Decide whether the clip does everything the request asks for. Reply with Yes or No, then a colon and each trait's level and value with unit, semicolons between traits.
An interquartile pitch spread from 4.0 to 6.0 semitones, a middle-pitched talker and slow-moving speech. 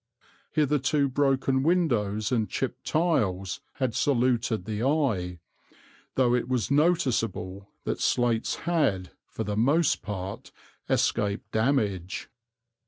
No: average, 5.3 semitones; low, 120 Hz; slow, 105 wpm